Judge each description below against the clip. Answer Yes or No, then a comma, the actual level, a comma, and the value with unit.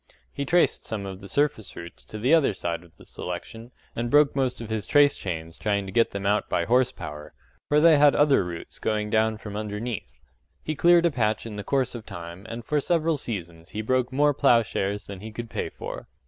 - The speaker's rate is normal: No, fast, 220 wpm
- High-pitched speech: No, low, 110 Hz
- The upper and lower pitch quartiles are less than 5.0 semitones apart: No, wide, 5.6 semitones